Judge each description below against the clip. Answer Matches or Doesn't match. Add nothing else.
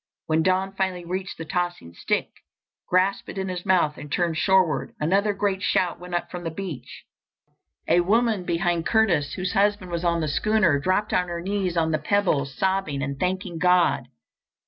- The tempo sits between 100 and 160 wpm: Doesn't match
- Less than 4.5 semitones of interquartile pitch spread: Matches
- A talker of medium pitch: Matches